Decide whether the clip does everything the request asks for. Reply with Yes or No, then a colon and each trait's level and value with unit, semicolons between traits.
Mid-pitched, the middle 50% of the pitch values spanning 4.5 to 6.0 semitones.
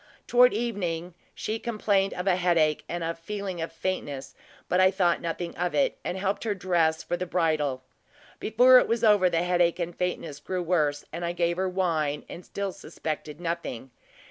No: medium, 175 Hz; average, 2.7 semitones